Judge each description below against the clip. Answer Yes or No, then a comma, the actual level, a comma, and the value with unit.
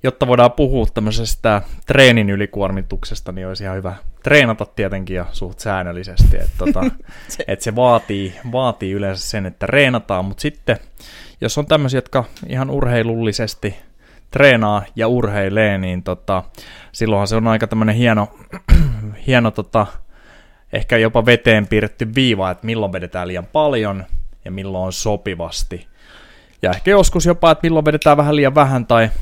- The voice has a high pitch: No, low, 110 Hz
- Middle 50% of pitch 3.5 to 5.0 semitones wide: Yes, average, 4.2 semitones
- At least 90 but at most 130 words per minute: No, average, 140 wpm